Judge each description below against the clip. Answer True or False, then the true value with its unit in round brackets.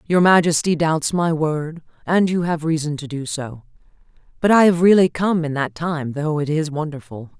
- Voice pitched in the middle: True (160 Hz)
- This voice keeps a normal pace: True (195 wpm)